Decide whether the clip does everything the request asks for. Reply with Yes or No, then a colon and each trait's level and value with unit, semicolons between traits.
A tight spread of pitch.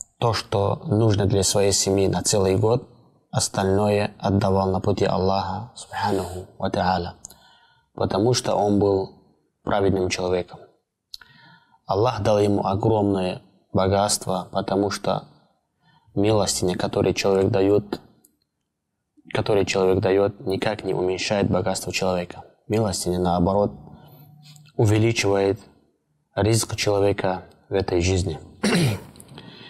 Yes: narrow, 1.6 semitones